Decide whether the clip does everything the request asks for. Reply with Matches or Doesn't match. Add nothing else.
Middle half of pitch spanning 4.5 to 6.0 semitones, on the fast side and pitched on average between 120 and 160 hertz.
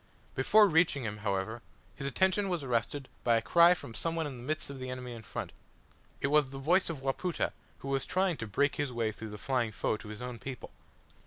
Matches